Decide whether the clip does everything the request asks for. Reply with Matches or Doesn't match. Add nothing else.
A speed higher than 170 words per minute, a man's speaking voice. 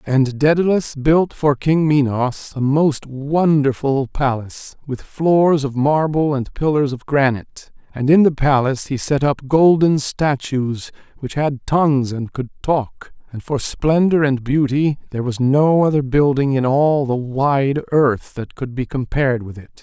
Doesn't match